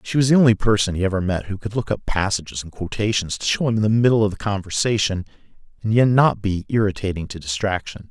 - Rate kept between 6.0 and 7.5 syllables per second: Yes, 6.4 syllables/s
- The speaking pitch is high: No, low, 105 Hz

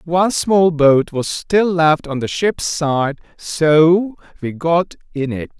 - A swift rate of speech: No, average, 160 wpm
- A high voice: No, medium, 160 Hz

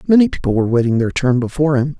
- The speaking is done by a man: Yes, male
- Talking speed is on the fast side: Yes, fast, 240 wpm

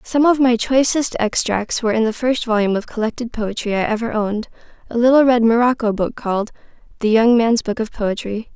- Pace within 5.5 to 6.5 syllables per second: Yes, 5.7 syllables/s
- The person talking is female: Yes, female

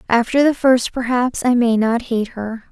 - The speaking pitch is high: Yes, high, 240 Hz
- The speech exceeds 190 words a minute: Yes, average, 200 wpm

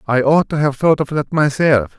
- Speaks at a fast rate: Yes, fast, 240 wpm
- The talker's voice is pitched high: No, medium, 140 Hz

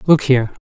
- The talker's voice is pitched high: No, low, 135 Hz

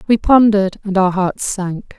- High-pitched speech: Yes, high, 200 Hz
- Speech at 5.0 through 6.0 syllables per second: No, 4.4 syllables/s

